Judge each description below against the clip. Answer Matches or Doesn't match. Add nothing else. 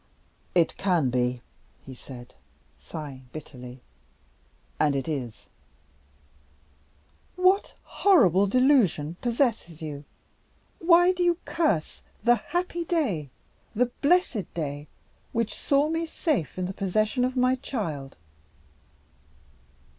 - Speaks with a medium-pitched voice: Doesn't match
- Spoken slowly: Matches